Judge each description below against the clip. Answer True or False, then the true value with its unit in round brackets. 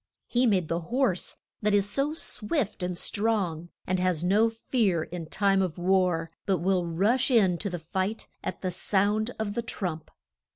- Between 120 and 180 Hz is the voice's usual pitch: False (190 Hz)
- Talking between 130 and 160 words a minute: False (175 wpm)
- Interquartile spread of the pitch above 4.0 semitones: False (3.7 semitones)